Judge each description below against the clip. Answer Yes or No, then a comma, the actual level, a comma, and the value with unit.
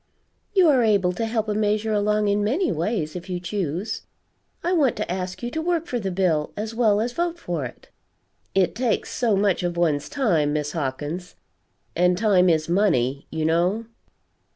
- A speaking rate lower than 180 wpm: No, average, 185 wpm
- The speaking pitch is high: Yes, high, 195 Hz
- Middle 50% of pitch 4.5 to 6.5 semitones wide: Yes, average, 4.8 semitones